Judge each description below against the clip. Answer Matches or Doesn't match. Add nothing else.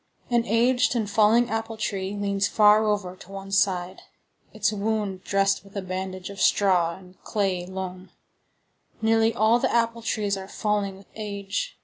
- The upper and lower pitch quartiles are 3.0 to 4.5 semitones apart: Doesn't match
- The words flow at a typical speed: Matches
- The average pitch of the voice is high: Matches